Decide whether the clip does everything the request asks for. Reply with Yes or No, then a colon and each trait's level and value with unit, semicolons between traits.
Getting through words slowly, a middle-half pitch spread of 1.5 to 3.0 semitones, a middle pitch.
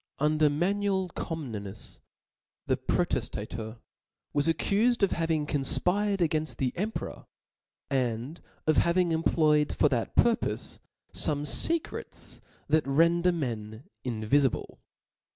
No: slow, 115 wpm; average, 4.9 semitones; medium, 155 Hz